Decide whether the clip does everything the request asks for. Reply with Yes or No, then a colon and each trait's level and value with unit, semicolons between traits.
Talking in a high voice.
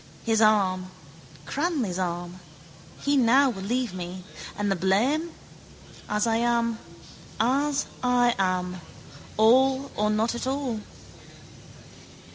Yes: high, 225 Hz